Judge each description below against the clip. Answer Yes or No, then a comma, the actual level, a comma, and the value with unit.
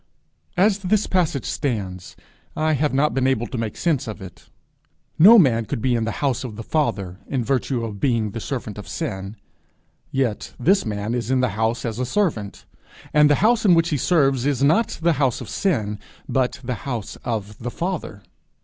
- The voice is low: Yes, low, 125 Hz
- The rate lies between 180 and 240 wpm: Yes, average, 195 wpm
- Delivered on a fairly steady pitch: No, average, 5.3 semitones